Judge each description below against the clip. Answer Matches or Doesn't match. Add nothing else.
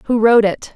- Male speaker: Doesn't match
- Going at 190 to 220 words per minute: Doesn't match